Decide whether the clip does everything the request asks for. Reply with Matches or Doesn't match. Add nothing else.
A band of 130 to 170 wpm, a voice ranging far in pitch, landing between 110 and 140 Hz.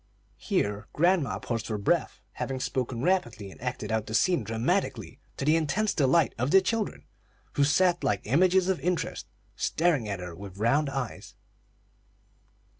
Matches